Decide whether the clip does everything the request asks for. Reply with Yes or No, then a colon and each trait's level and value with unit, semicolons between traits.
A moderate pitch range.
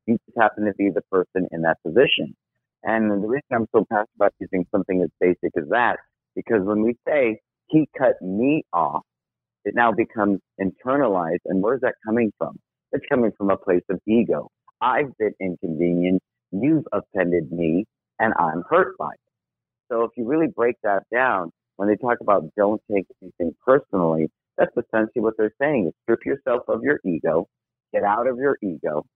Yes: average, 4.0 semitones